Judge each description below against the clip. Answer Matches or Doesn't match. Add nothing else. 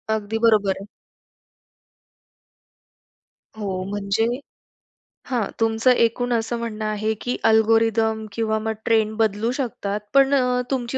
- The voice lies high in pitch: Matches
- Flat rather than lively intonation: Matches